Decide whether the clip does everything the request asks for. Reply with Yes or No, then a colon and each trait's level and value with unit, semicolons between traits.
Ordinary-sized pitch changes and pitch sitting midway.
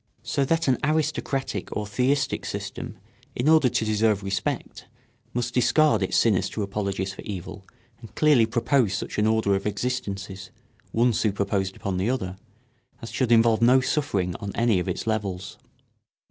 No: average, 4.3 semitones; low, 110 Hz